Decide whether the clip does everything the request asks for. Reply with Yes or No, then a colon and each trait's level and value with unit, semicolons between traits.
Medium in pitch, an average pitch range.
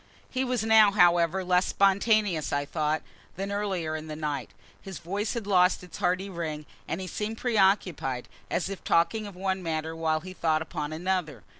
Yes: medium, 180 Hz; average, 4.0 semitones